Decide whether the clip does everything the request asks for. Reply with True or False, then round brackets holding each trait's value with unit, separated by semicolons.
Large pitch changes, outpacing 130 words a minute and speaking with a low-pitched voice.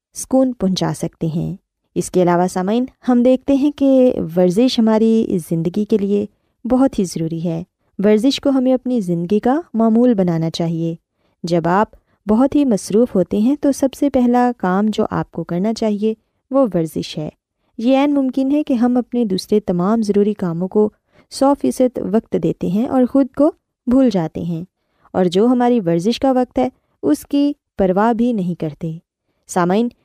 False (6.0 semitones; 175 wpm; 220 Hz)